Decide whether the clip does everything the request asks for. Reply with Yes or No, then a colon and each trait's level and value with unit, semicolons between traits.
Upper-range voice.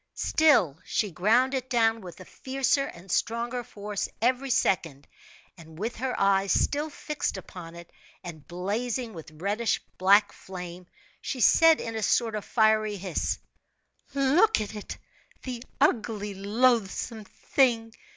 Yes: high, 215 Hz